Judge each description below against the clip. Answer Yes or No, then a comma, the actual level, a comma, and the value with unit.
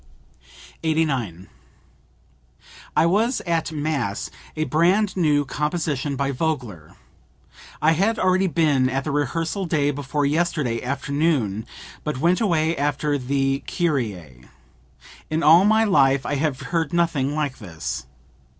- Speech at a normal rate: No, slow, 125 wpm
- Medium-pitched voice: Yes, medium, 150 Hz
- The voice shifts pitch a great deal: No, average, 3.6 semitones